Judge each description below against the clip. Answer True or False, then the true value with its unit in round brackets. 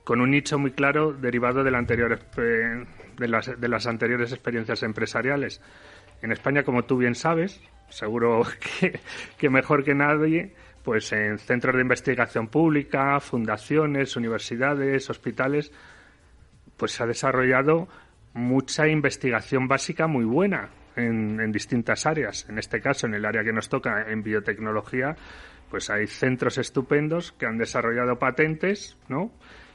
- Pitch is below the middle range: True (130 Hz)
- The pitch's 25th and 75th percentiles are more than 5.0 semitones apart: False (3.7 semitones)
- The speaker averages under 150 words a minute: True (140 wpm)